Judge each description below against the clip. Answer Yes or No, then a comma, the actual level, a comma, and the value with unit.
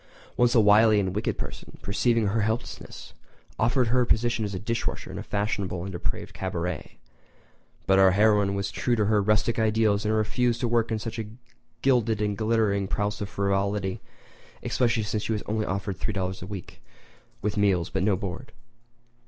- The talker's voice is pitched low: Yes, low, 105 Hz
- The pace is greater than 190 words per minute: No, average, 175 wpm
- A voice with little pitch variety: Yes, narrow, 2.3 semitones